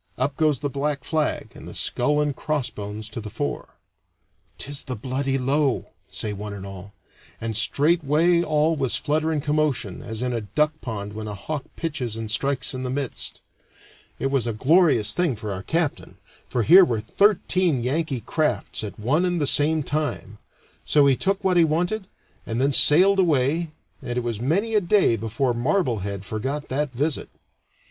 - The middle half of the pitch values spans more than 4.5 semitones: Yes, average, 5.3 semitones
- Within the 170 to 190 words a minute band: Yes, average, 180 wpm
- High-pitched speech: No, medium, 140 Hz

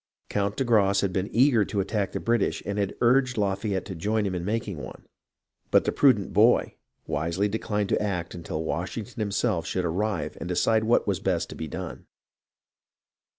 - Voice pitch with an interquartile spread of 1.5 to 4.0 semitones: Yes, average, 3.1 semitones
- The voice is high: No, low, 100 Hz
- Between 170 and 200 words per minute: Yes, average, 185 wpm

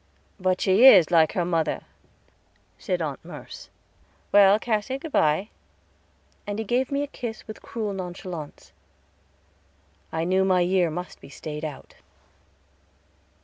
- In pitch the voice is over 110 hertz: Yes, high, 190 Hz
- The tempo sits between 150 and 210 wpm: No, slow, 135 wpm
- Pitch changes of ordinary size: Yes, average, 4.1 semitones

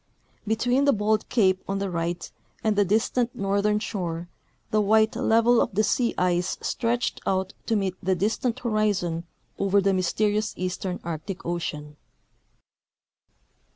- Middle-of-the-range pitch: No, high, 200 Hz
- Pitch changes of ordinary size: Yes, average, 3.1 semitones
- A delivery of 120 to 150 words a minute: Yes, average, 140 wpm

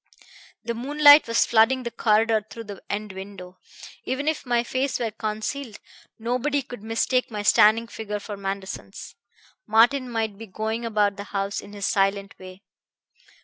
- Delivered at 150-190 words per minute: Yes, average, 155 wpm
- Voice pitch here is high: Yes, high, 220 Hz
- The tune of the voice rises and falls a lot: No, average, 3.0 semitones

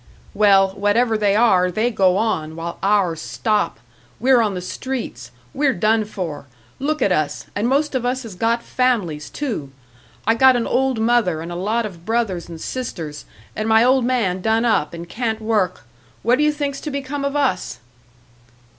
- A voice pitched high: Yes, high, 220 Hz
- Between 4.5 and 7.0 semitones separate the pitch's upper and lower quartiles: Yes, wide, 5.5 semitones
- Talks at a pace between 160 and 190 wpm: Yes, average, 180 wpm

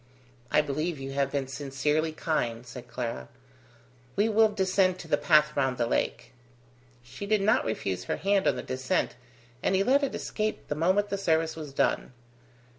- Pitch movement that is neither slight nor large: No, wide, 6.7 semitones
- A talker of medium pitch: Yes, medium, 155 Hz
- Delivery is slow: No, average, 180 wpm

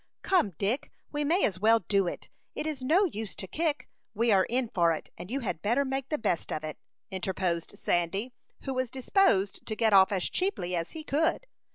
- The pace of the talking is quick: Yes, fast, 210 wpm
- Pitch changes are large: Yes, wide, 6.9 semitones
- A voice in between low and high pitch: No, high, 225 Hz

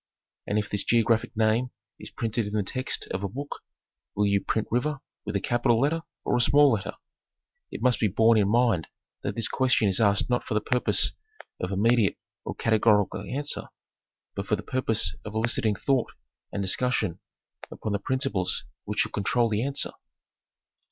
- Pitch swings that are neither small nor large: Yes, average, 3.2 semitones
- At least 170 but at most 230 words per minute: Yes, average, 180 wpm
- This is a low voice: Yes, low, 110 Hz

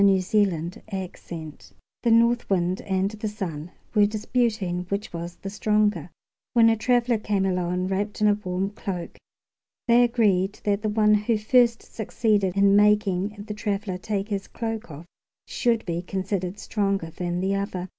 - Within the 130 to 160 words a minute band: Yes, average, 155 wpm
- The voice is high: Yes, high, 200 Hz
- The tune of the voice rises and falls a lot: No, average, 2.8 semitones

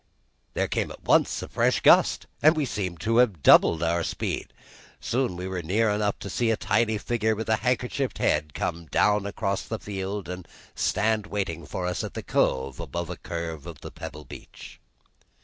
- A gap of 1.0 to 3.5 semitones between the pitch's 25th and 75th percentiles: No, average, 4.5 semitones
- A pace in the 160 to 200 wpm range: Yes, average, 185 wpm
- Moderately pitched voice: No, low, 100 Hz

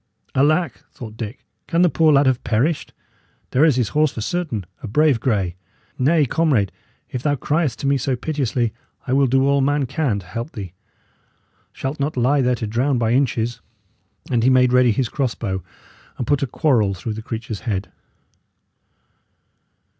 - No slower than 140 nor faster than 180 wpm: Yes, average, 175 wpm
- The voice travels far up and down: No, average, 4.1 semitones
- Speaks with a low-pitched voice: Yes, low, 125 Hz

